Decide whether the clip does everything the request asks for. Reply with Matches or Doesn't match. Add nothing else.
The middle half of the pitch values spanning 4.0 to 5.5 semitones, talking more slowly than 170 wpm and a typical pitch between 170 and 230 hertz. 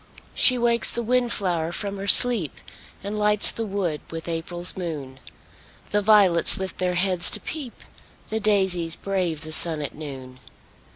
Matches